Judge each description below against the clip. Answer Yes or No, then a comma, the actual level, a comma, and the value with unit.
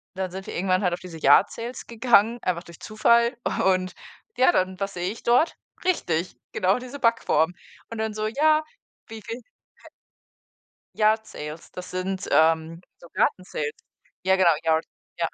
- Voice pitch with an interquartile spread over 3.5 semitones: Yes, average, 4.5 semitones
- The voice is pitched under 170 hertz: No, high, 190 Hz